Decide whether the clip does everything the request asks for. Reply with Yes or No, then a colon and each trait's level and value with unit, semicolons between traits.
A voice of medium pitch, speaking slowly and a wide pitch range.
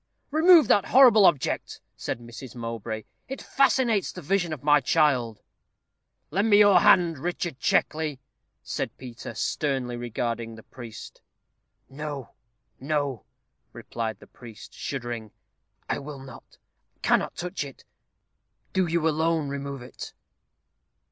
Yes: medium, 145 Hz; slow, 120 wpm; wide, 6.4 semitones